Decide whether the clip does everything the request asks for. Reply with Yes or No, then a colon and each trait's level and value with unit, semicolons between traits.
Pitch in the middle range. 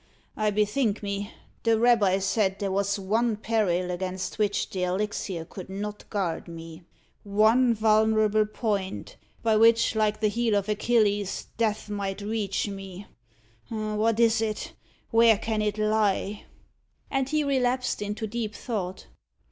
No: high, 210 Hz